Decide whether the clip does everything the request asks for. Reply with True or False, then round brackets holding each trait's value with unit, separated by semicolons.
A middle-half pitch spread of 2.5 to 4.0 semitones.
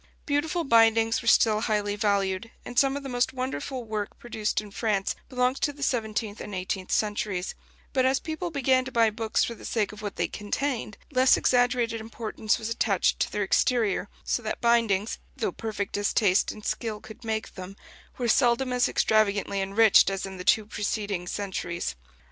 True (3.2 semitones)